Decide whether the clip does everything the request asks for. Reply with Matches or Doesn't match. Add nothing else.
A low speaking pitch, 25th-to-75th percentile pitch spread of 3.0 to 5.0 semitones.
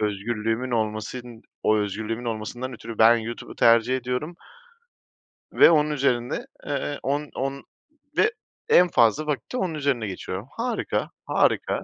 Matches